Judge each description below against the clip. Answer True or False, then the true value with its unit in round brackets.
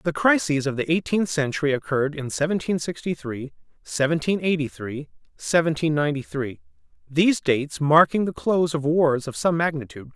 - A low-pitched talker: False (145 Hz)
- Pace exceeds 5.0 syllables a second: True (5.5 syllables/s)